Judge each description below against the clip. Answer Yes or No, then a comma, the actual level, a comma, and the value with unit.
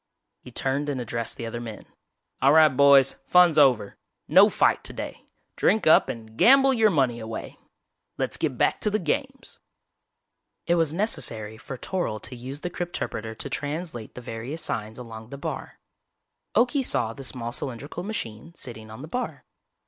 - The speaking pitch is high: No, low, 135 Hz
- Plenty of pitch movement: Yes, wide, 6.9 semitones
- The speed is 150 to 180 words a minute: Yes, average, 165 wpm